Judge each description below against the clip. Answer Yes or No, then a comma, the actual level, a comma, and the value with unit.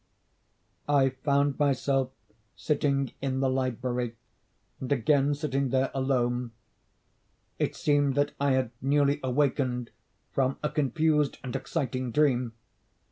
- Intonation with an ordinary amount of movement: No, narrow, 2.0 semitones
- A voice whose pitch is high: No, low, 135 Hz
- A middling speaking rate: No, slow, 115 wpm